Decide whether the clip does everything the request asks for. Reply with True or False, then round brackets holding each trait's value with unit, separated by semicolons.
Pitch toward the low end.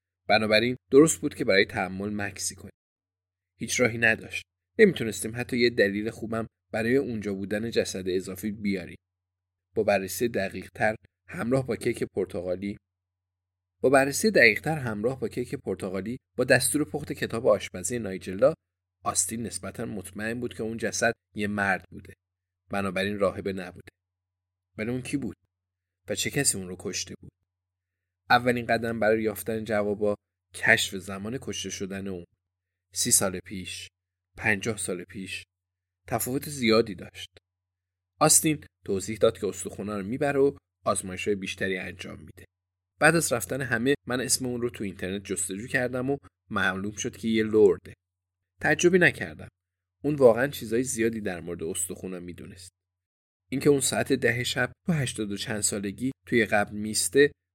True (100 Hz)